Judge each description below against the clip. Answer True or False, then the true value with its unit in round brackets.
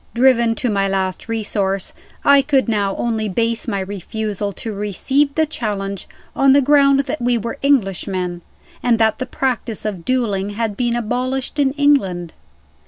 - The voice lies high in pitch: True (225 Hz)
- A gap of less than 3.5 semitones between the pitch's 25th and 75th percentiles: False (4.8 semitones)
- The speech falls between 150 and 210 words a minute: True (160 wpm)